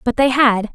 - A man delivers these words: No, female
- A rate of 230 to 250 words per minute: Yes, fast, 240 wpm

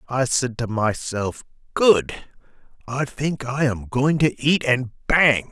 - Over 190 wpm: No, average, 150 wpm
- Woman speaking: No, male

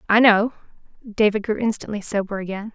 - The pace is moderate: Yes, average, 155 wpm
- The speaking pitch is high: Yes, high, 210 Hz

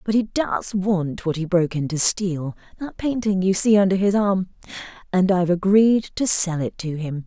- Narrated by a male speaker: No, female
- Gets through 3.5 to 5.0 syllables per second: Yes, 4.8 syllables/s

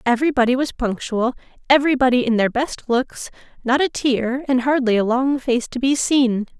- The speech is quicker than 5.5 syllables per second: No, 5.2 syllables/s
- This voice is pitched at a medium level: No, very high, 255 Hz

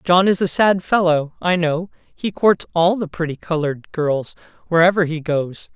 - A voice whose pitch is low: No, medium, 170 Hz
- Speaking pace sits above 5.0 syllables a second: No, 4.5 syllables/s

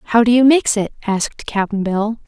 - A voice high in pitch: Yes, high, 220 Hz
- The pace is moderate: No, fast, 210 wpm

